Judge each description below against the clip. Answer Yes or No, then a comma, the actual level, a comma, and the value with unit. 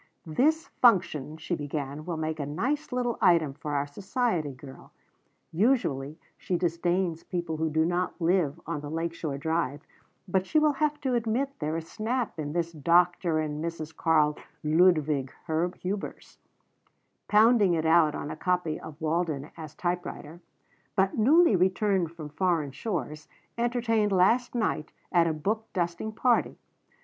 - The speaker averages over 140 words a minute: Yes, average, 155 wpm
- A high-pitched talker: No, medium, 170 Hz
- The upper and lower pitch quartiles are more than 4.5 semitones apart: Yes, average, 5.0 semitones